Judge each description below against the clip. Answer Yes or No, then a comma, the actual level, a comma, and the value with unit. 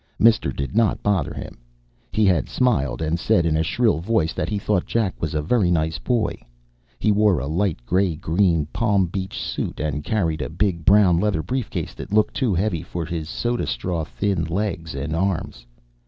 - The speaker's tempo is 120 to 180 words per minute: No, average, 190 wpm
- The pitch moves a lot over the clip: No, average, 4.7 semitones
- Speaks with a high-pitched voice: No, very low, 90 Hz